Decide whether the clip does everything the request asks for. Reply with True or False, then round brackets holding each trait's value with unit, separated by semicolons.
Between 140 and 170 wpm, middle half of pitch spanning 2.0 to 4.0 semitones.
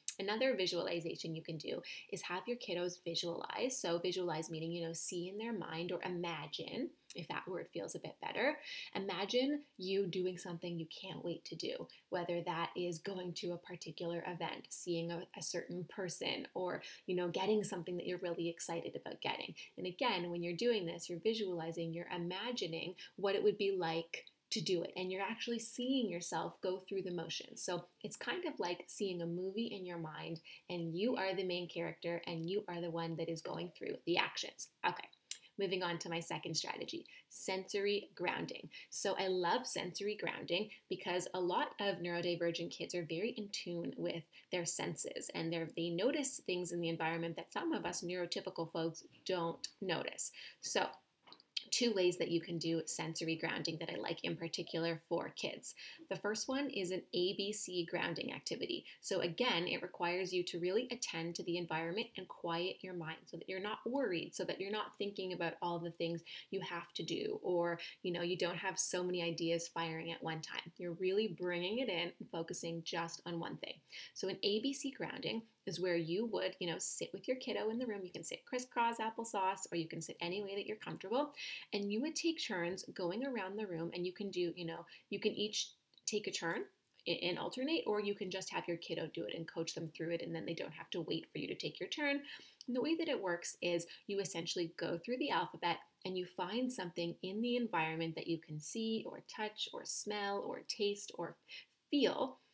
False (205 wpm; 3.4 semitones)